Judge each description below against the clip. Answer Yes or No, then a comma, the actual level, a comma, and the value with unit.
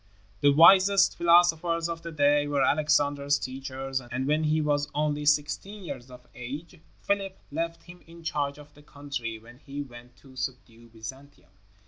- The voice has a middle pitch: Yes, medium, 145 Hz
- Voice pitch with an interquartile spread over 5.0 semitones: No, average, 3.7 semitones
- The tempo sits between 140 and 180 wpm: Yes, average, 160 wpm